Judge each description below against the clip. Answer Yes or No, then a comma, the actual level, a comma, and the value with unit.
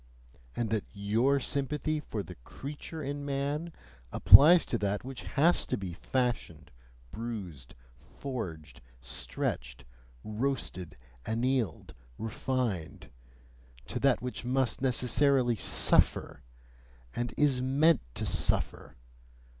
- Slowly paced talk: Yes, slow, 105 wpm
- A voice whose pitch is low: Yes, low, 125 Hz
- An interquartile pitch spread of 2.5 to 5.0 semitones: No, wide, 5.5 semitones